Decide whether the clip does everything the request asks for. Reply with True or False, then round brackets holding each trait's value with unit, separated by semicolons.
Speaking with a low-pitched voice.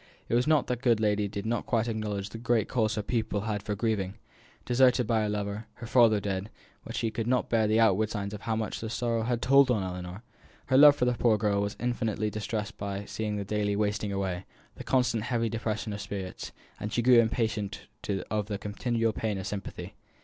True (110 Hz)